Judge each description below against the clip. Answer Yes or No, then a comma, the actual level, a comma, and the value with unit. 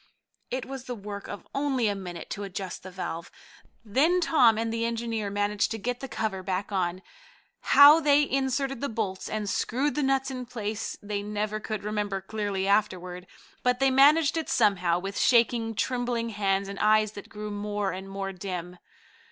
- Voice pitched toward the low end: No, high, 215 Hz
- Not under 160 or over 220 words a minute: Yes, average, 180 wpm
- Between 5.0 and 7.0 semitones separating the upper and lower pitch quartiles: No, average, 4.1 semitones